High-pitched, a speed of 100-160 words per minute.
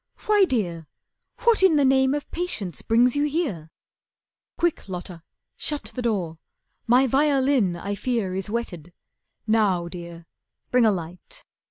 Yes: high, 225 Hz; average, 140 wpm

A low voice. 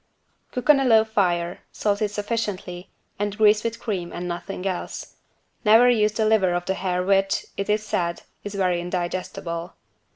No: high, 195 Hz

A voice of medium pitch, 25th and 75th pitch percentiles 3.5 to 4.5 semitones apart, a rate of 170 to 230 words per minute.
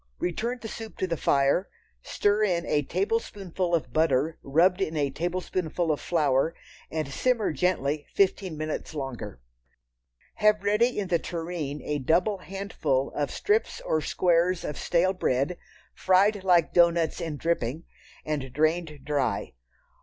No: medium, 170 Hz; average, 4.0 semitones; average, 140 wpm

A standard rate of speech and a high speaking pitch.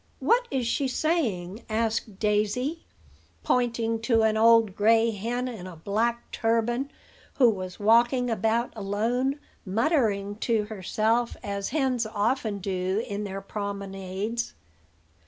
No: slow, 120 wpm; high, 225 Hz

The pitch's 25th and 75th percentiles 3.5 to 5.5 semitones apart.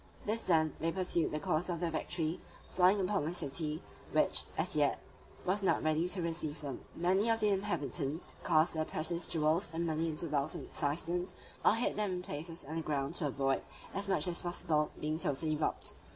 No: average, 2.7 semitones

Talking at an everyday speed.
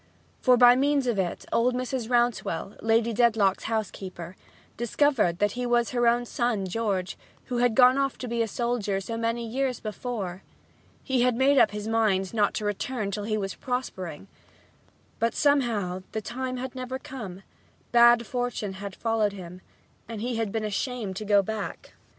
Yes: average, 175 wpm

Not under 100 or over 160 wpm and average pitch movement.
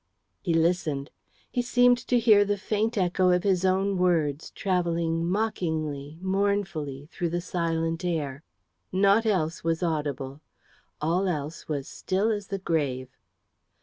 Yes: slow, 135 wpm; average, 3.9 semitones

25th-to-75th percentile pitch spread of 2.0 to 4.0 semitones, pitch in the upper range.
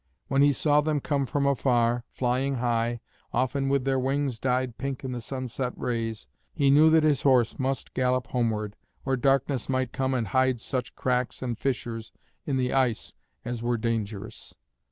No: narrow, 2.4 semitones; low, 130 Hz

